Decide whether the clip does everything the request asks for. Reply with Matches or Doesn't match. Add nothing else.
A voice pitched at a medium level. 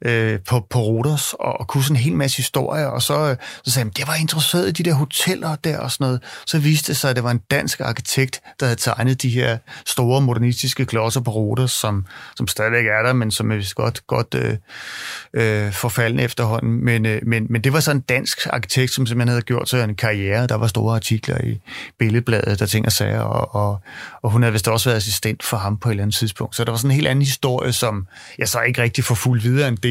Doesn't match